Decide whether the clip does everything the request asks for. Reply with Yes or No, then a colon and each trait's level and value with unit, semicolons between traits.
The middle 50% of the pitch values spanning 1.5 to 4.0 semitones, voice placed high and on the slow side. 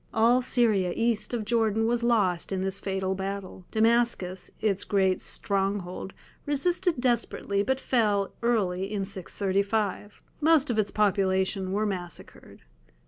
Yes: average, 3.4 semitones; high, 205 Hz; slow, 130 wpm